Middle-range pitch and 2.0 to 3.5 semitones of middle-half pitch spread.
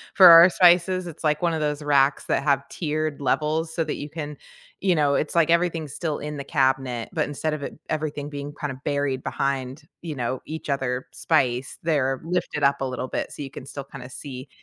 Yes: medium, 145 Hz; average, 2.8 semitones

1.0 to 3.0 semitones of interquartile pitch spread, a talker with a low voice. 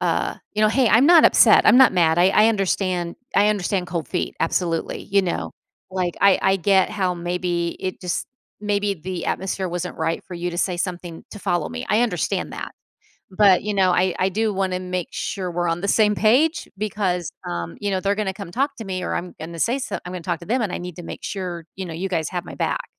No: average, 2.7 semitones; medium, 185 Hz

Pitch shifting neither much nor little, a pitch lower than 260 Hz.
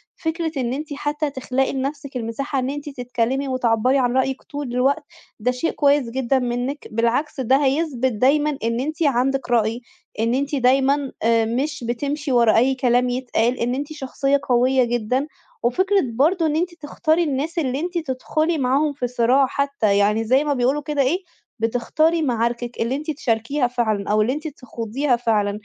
No: average, 3.4 semitones; very high, 265 Hz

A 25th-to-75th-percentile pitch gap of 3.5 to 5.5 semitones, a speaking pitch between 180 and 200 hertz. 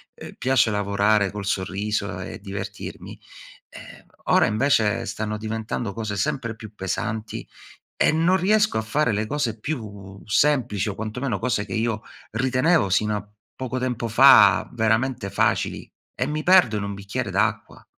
No: average, 3.9 semitones; low, 110 Hz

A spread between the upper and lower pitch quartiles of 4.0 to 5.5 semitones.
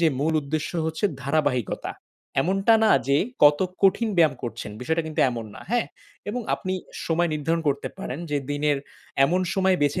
Yes: average, 4.4 semitones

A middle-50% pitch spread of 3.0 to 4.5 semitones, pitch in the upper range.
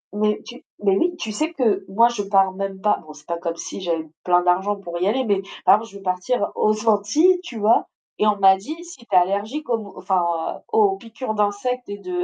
Yes: average, 4.0 semitones; high, 205 Hz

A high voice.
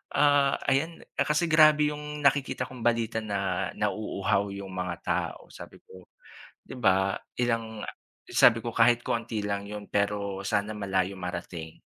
No: low, 110 Hz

